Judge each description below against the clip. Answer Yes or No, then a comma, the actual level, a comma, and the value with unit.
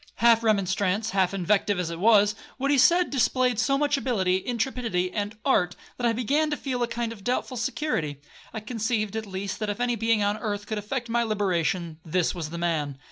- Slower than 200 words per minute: No, fast, 205 wpm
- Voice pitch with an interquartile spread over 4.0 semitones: Yes, average, 4.5 semitones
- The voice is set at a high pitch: Yes, high, 215 Hz